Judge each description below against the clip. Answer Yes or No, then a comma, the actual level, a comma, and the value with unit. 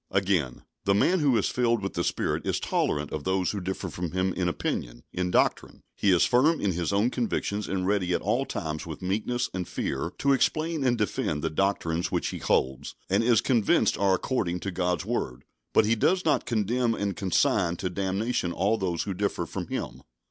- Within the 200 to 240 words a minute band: Yes, fast, 205 wpm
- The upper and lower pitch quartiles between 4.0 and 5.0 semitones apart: Yes, average, 4.6 semitones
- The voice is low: Yes, very low, 95 Hz